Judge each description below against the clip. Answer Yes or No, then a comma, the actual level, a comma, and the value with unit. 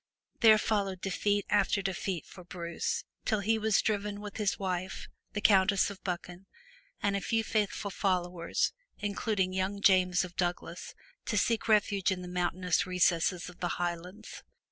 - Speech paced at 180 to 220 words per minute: No, average, 155 wpm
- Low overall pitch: No, high, 190 Hz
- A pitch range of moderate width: No, narrow, 2.3 semitones